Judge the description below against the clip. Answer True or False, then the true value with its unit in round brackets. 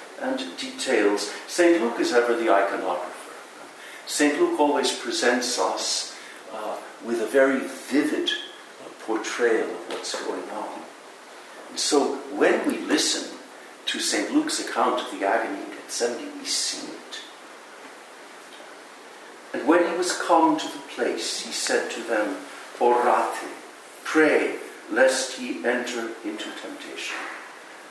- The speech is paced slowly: True (130 wpm)